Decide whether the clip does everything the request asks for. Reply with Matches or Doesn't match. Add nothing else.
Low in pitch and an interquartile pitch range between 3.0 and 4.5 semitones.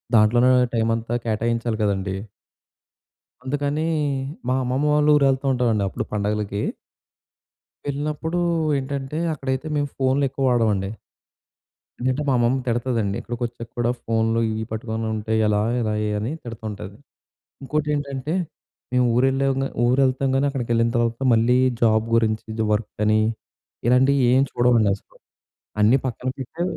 Matches